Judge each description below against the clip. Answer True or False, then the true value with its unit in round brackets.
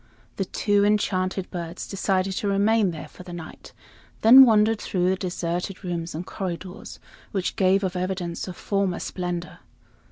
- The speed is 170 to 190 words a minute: False (155 wpm)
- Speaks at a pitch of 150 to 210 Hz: True (185 Hz)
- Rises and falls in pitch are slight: True (2.2 semitones)